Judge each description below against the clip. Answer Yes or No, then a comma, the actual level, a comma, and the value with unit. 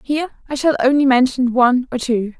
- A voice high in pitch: Yes, very high, 260 Hz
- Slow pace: No, average, 200 wpm